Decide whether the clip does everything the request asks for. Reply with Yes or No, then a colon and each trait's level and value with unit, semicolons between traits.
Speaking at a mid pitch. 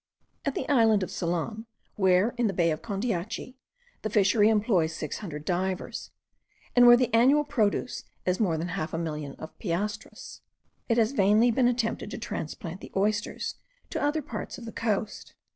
No: high, 210 Hz